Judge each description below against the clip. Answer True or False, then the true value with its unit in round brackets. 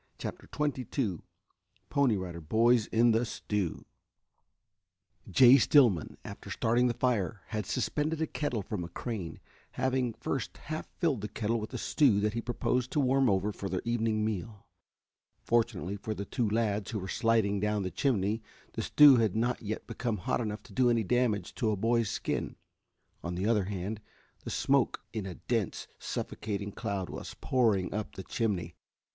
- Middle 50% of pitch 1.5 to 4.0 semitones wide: True (3.4 semitones)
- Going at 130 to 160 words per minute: False (170 wpm)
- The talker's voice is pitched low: True (110 Hz)